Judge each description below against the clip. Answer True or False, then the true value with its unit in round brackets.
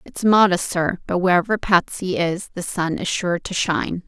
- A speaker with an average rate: True (190 wpm)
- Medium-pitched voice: True (180 Hz)